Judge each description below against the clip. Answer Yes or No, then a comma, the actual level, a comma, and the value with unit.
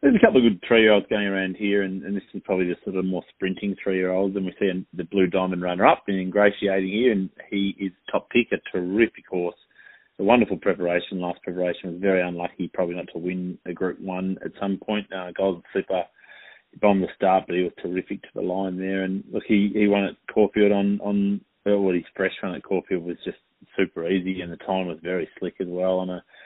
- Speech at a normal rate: No, fast, 225 wpm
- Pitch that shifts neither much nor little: No, narrow, 1.7 semitones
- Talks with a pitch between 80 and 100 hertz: Yes, very low, 95 Hz